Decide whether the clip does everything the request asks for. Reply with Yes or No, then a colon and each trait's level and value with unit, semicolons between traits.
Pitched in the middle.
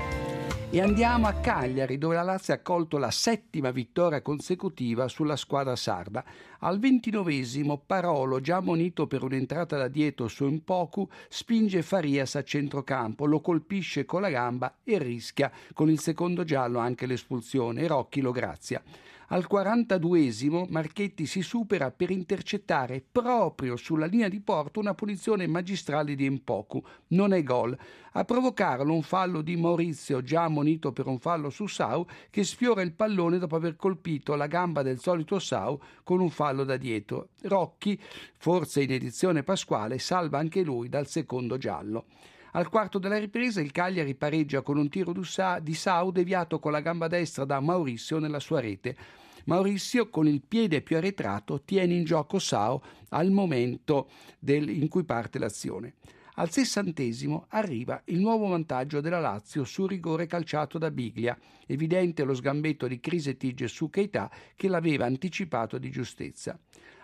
Yes: medium, 160 Hz